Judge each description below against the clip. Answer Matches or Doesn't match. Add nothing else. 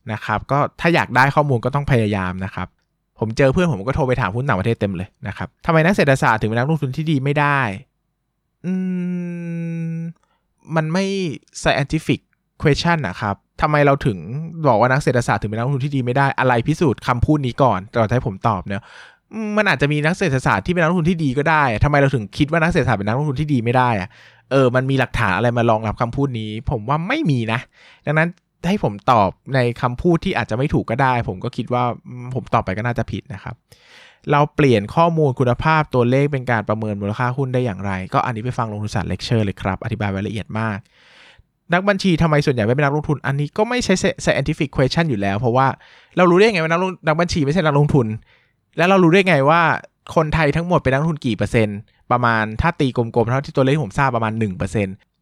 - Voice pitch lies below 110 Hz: Doesn't match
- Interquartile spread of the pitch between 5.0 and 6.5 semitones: Matches